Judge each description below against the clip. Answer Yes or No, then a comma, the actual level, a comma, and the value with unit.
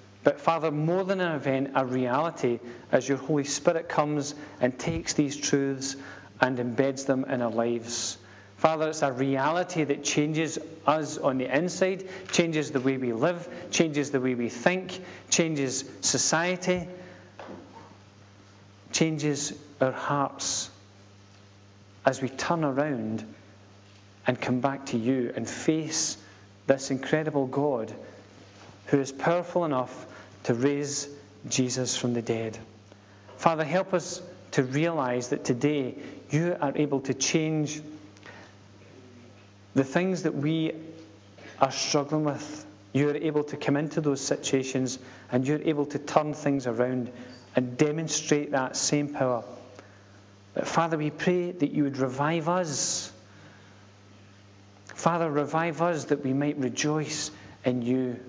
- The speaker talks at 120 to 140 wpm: Yes, slow, 135 wpm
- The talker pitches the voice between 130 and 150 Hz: Yes, low, 135 Hz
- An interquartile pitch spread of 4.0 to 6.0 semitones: Yes, average, 4.7 semitones